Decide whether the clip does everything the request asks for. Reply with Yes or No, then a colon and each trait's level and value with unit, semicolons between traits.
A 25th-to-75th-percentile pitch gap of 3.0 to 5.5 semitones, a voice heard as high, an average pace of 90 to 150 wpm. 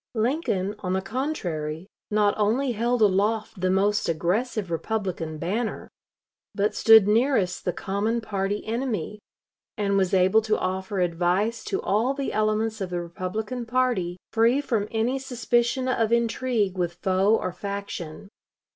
Yes: average, 3.8 semitones; high, 210 Hz; average, 140 wpm